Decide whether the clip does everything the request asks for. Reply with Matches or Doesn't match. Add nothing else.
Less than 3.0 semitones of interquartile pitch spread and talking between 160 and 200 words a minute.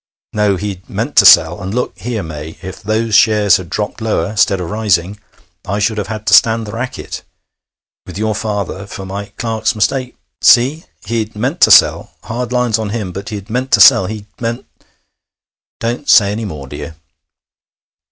Matches